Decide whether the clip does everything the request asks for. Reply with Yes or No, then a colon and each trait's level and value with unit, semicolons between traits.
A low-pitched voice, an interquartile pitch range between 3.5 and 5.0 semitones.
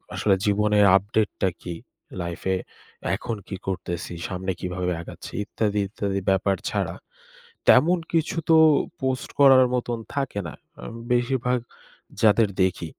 Yes: low, 105 Hz; average, 4.6 semitones